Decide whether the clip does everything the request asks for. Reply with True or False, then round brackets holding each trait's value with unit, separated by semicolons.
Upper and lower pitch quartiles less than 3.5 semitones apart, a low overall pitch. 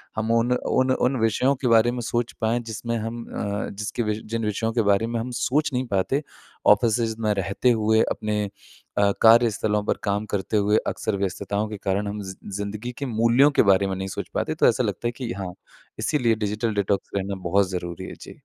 True (2.5 semitones; 110 Hz)